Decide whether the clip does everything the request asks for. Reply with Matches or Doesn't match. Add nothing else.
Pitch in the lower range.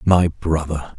Matches